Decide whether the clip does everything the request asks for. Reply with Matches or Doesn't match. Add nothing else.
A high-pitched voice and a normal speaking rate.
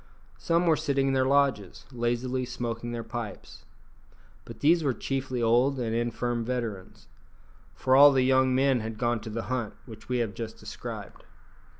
Doesn't match